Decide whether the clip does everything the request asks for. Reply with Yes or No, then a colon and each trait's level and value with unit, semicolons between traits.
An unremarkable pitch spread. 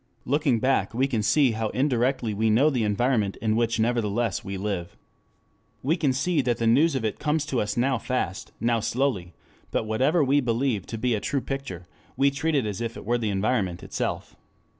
Yes: average, 4.0 semitones